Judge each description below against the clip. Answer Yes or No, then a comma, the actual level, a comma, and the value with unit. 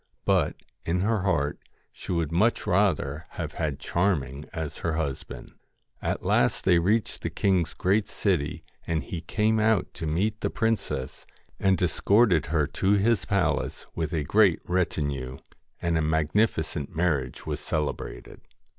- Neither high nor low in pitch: No, very low, 85 Hz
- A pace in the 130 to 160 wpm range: Yes, average, 150 wpm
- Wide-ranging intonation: No, average, 4.6 semitones